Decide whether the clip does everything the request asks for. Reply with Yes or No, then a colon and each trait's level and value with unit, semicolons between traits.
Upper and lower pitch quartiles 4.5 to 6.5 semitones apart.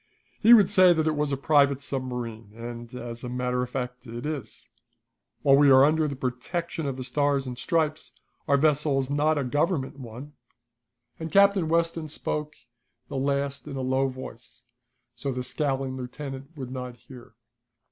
No: average, 3.2 semitones